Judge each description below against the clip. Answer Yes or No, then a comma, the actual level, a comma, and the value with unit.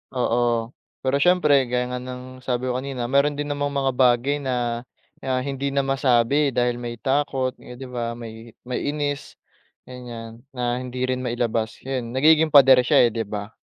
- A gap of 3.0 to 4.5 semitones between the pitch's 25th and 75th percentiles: No, narrow, 2.4 semitones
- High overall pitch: No, low, 125 Hz